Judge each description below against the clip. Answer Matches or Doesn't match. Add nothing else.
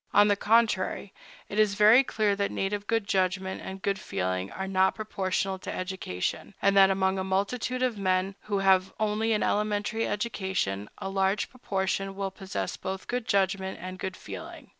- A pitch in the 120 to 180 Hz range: Doesn't match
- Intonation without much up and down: Matches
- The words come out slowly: Doesn't match